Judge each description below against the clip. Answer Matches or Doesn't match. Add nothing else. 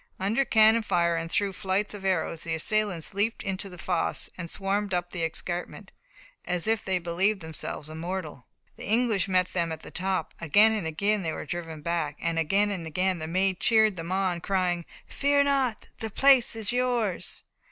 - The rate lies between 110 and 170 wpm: Doesn't match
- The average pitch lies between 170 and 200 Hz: Matches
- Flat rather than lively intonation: Doesn't match